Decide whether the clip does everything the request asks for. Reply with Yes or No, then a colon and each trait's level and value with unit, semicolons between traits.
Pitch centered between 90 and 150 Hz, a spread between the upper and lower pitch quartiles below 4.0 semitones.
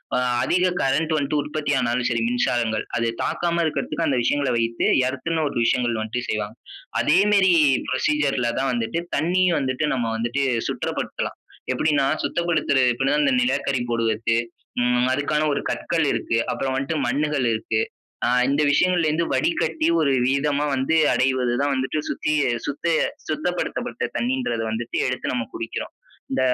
No: low, 135 Hz; average, 4.3 semitones